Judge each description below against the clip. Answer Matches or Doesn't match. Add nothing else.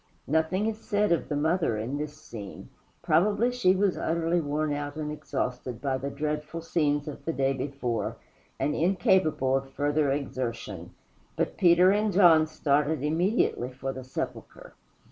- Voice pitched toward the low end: Doesn't match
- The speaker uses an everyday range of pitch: Matches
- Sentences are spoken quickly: Doesn't match